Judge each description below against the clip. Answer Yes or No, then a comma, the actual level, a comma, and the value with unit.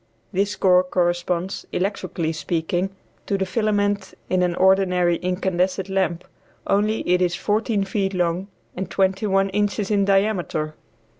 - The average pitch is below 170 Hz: No, high, 190 Hz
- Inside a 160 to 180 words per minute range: No, slow, 135 wpm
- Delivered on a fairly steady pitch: Yes, narrow, 1.9 semitones